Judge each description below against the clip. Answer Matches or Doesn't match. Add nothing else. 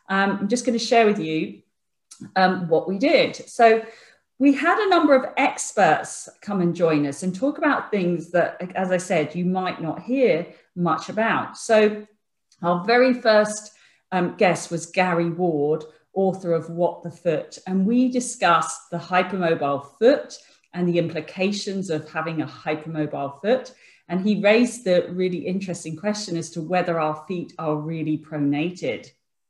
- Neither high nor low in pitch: Matches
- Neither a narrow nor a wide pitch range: Matches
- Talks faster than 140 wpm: Matches